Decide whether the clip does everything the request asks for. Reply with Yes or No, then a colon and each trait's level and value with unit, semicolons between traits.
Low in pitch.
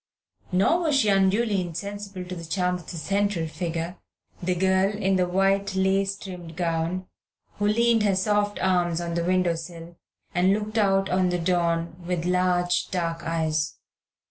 No: medium, 185 Hz